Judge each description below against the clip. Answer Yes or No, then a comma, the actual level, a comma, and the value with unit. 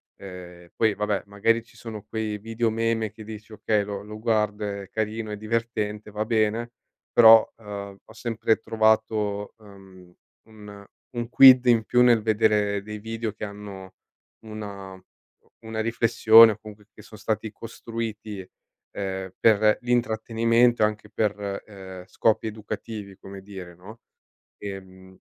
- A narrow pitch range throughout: Yes, narrow, 1.9 semitones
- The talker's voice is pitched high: No, low, 105 Hz